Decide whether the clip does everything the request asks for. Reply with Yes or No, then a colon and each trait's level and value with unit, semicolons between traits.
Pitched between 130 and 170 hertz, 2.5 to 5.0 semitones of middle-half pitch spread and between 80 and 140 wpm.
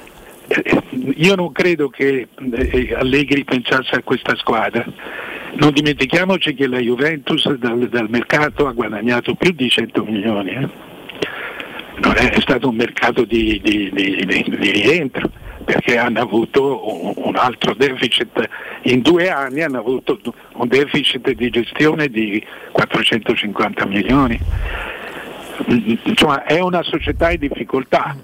Yes: low, 135 Hz; average, 3.7 semitones; average, 120 wpm